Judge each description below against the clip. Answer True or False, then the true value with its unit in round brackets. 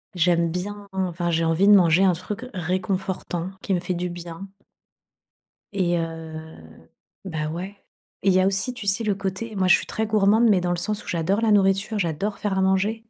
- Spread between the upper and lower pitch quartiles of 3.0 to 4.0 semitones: False (2.6 semitones)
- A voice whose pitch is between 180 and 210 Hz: True (190 Hz)